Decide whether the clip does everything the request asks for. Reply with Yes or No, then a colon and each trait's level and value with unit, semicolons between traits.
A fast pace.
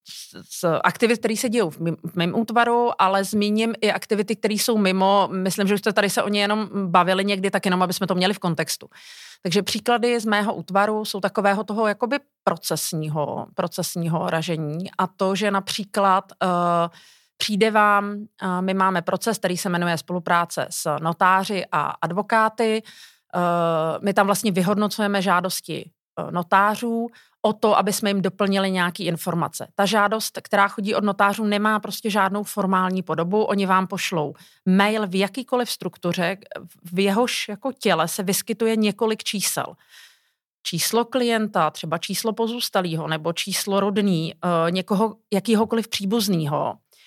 No: average, 150 wpm